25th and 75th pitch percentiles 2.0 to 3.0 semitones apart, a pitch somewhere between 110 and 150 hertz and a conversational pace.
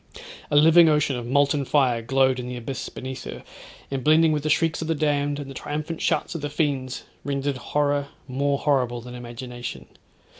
Yes: narrow, 2.5 semitones; medium, 140 Hz; average, 190 wpm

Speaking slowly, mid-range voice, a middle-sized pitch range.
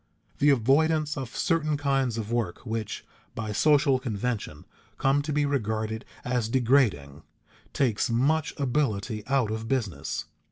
No: slow, 130 wpm; low, 125 Hz; average, 4.4 semitones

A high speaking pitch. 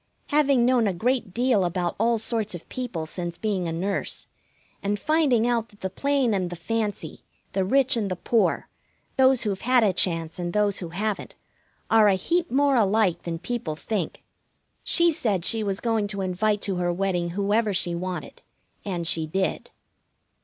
Yes: high, 205 Hz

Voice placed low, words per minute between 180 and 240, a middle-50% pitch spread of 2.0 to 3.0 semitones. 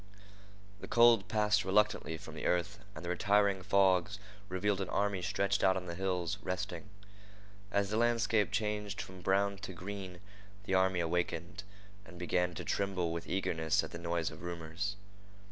No: very low, 95 Hz; average, 160 wpm; narrow, 2.5 semitones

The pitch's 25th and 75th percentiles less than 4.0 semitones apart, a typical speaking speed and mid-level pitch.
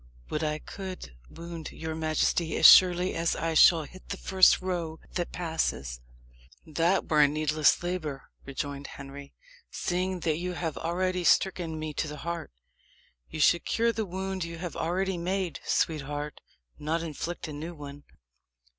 Yes: average, 2.9 semitones; average, 155 wpm; medium, 165 Hz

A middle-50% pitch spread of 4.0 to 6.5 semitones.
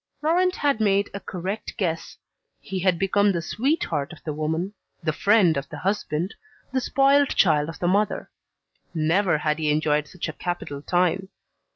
Yes: average, 4.6 semitones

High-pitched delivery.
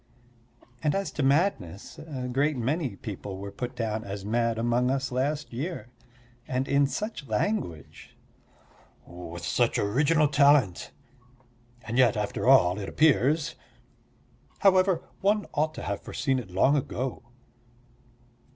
No: low, 130 Hz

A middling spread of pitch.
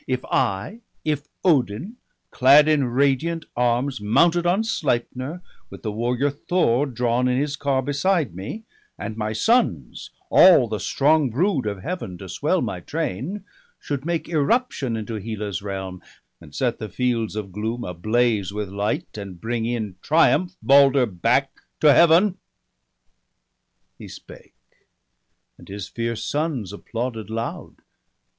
No: wide, 5.8 semitones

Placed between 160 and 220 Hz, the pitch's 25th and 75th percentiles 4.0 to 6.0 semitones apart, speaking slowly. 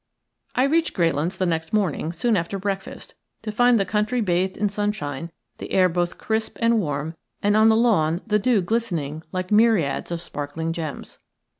No: high, 190 Hz; average, 4.9 semitones; average, 175 wpm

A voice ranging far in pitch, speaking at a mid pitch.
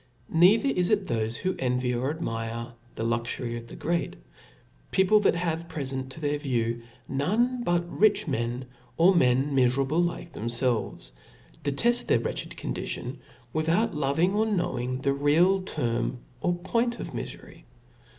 Yes: wide, 6.3 semitones; medium, 145 Hz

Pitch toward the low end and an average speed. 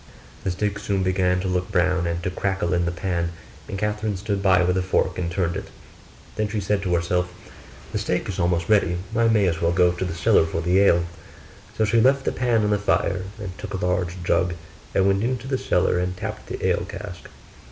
No: very low, 95 Hz; fast, 225 wpm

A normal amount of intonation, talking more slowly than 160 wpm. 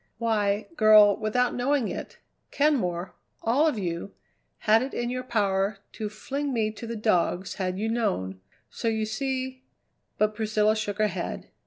No: average, 3.0 semitones; average, 165 wpm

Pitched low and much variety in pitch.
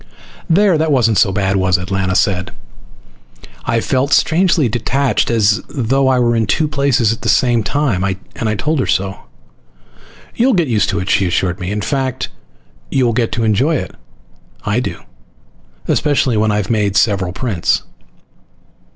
Yes: low, 115 Hz; wide, 5.7 semitones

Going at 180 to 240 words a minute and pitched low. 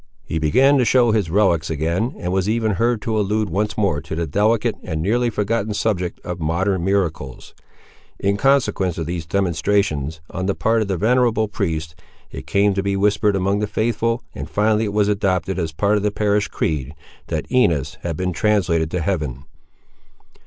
Yes: average, 185 wpm; low, 100 Hz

